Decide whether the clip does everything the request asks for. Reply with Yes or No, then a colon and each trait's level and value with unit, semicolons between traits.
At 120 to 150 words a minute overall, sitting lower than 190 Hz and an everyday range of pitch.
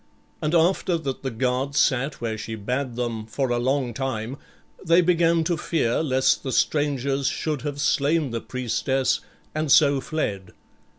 No: average, 160 wpm; low, 135 Hz; average, 4.0 semitones